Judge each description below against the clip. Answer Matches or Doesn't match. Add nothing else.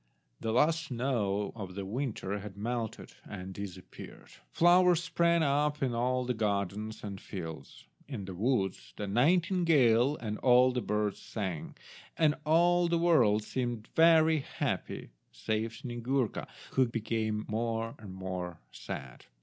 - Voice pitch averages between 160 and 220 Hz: Doesn't match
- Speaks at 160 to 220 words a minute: Doesn't match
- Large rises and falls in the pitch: Matches